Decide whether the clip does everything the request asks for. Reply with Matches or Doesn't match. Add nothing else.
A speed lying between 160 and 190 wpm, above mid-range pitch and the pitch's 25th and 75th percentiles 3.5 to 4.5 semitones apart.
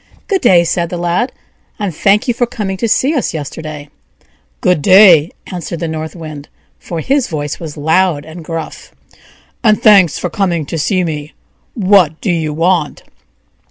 Doesn't match